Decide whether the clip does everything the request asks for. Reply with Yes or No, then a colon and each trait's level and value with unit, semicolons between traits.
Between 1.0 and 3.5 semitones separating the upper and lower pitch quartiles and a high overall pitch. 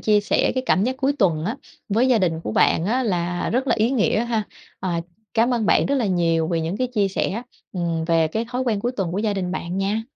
No: average, 5.3 semitones; high, 205 Hz